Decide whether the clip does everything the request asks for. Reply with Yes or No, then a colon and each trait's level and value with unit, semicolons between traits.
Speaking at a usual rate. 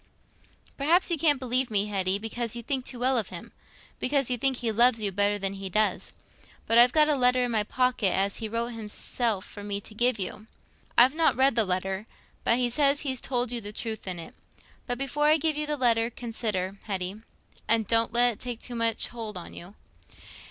No: fast, 215 wpm